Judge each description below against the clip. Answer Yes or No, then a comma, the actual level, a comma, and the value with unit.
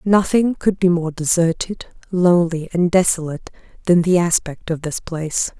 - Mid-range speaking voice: Yes, medium, 175 Hz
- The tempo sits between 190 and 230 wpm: No, average, 150 wpm